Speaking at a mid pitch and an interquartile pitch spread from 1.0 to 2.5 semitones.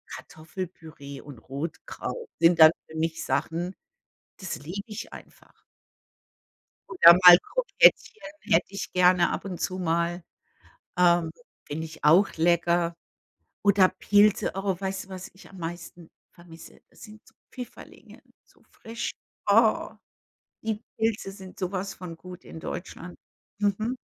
No: medium, 180 Hz; average, 2.9 semitones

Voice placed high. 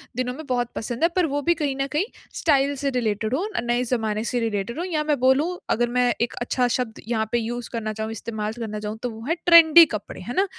Yes: high, 245 Hz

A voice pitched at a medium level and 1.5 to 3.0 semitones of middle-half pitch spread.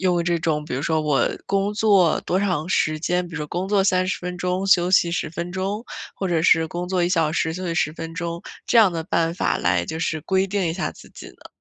Yes: medium, 175 Hz; narrow, 2.6 semitones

